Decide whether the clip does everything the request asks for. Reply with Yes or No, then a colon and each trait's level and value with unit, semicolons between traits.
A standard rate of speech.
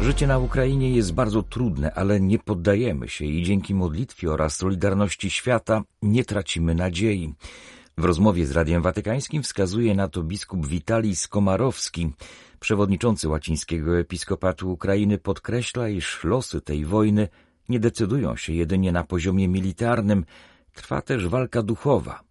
Yes: average, 135 wpm